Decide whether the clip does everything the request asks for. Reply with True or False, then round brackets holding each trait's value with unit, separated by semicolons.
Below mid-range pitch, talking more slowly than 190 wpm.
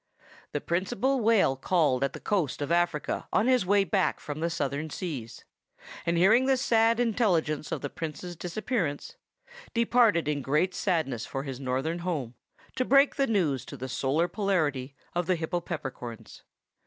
False (170 Hz; 160 wpm)